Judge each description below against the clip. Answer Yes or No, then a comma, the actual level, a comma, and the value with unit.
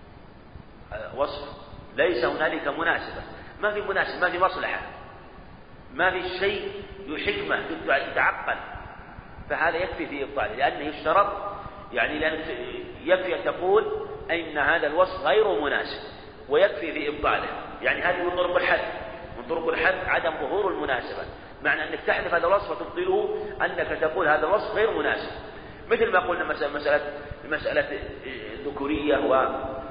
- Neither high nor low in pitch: Yes, medium, 180 Hz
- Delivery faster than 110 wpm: Yes, average, 125 wpm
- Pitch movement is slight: No, wide, 5.5 semitones